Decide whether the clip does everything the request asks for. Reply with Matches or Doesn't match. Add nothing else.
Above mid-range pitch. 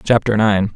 Doesn't match